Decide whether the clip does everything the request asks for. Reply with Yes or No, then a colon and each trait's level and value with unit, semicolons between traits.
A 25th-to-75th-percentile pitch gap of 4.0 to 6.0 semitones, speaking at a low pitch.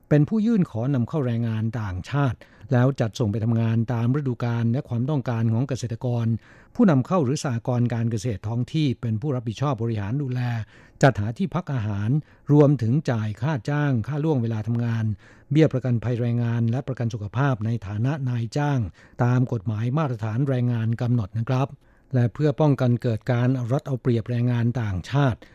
No: average, 3.2 semitones; low, 125 Hz